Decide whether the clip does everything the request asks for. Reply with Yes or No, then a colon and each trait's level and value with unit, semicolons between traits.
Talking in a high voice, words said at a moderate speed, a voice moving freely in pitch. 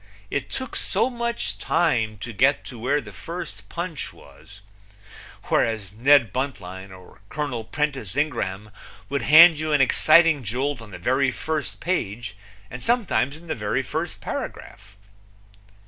No: low, 130 Hz; average, 145 wpm; wide, 6.4 semitones